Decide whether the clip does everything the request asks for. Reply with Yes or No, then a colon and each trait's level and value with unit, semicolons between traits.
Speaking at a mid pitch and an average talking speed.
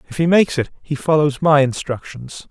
Yes: medium, 145 Hz; average, 190 wpm